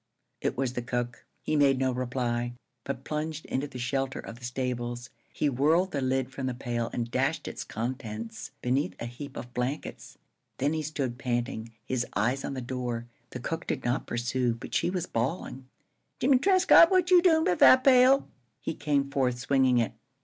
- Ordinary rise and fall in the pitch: Yes, average, 3.4 semitones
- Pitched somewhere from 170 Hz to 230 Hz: No, low, 130 Hz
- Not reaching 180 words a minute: No, average, 185 wpm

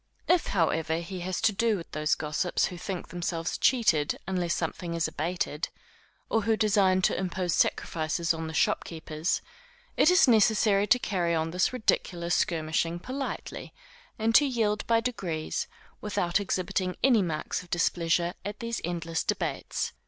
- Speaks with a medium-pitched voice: Yes, medium, 180 Hz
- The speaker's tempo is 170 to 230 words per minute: No, average, 150 wpm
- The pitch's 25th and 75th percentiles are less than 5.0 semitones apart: Yes, average, 4.2 semitones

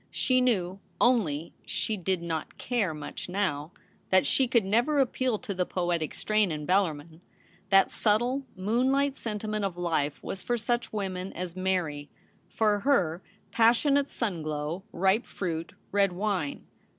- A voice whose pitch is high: Yes, high, 195 Hz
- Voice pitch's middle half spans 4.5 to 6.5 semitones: Yes, average, 5.2 semitones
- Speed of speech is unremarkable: Yes, average, 155 wpm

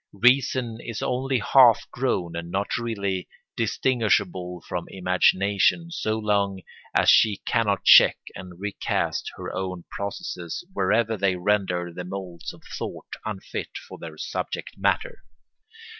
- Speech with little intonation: No, average, 3.8 semitones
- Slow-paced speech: Yes, slow, 130 wpm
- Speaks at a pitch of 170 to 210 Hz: No, low, 100 Hz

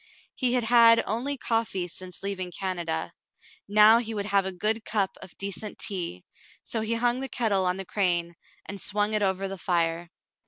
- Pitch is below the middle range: No, high, 200 Hz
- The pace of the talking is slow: No, average, 185 wpm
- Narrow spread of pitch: No, average, 3.5 semitones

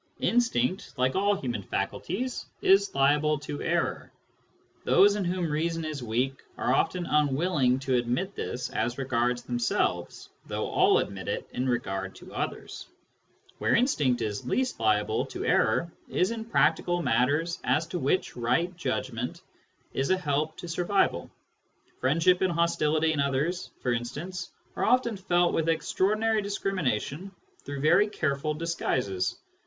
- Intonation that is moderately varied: No, wide, 6.1 semitones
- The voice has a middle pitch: Yes, medium, 150 Hz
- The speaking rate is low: No, average, 145 wpm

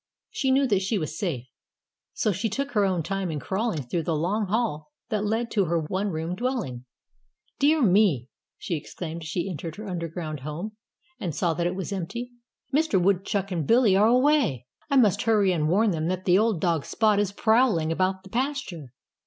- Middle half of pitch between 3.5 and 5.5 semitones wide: Yes, average, 5.0 semitones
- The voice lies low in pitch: No, high, 190 Hz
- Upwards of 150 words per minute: Yes, average, 195 wpm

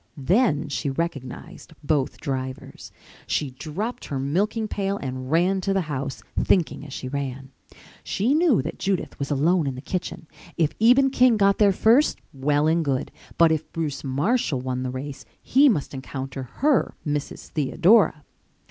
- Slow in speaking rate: No, average, 160 wpm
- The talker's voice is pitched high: No, medium, 155 Hz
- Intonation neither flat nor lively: No, wide, 6.5 semitones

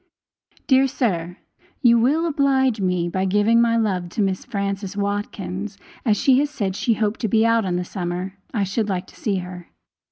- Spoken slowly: No, average, 190 wpm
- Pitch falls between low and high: No, high, 205 Hz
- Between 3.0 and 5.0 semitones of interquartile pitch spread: Yes, average, 3.8 semitones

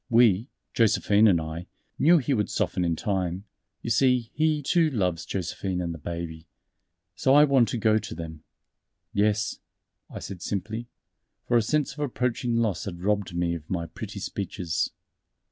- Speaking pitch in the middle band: No, low, 105 Hz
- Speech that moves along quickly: No, average, 165 wpm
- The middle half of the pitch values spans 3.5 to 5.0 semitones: No, wide, 5.6 semitones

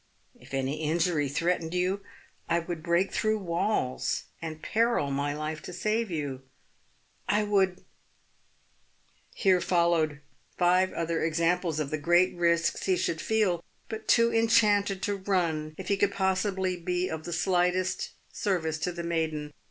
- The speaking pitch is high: No, medium, 175 Hz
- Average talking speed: Yes, average, 150 wpm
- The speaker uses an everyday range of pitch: Yes, average, 3.2 semitones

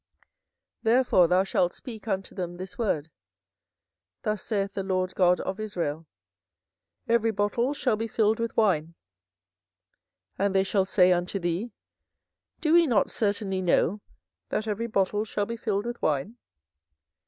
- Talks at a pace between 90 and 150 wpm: Yes, average, 145 wpm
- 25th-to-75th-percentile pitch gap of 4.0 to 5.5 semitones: No, average, 3.3 semitones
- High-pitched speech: Yes, high, 200 Hz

